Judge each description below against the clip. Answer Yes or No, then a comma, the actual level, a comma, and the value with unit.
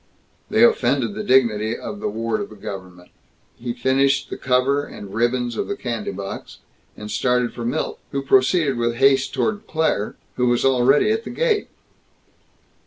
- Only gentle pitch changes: No, average, 3.3 semitones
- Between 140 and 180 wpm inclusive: Yes, average, 170 wpm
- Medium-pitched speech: No, low, 125 Hz